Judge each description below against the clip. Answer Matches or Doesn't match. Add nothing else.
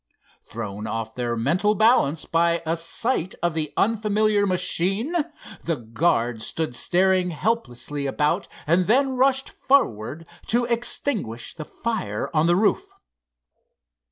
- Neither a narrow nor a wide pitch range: Doesn't match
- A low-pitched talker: Doesn't match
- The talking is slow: Matches